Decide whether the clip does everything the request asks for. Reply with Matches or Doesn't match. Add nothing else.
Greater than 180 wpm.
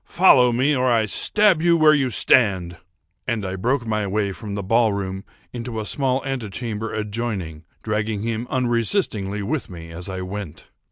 Doesn't match